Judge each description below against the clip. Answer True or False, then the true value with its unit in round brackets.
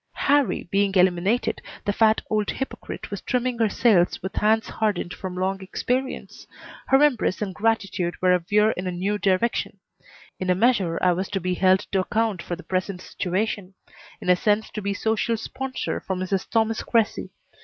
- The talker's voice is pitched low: False (200 Hz)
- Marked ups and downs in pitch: False (3.3 semitones)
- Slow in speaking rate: False (180 wpm)